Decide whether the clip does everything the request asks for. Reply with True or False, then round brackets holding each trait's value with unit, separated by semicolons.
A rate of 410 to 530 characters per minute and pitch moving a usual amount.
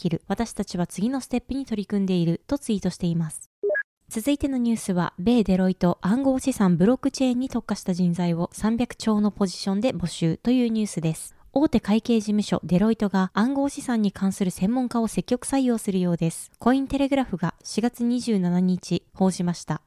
False (395 characters per minute; 5.0 semitones)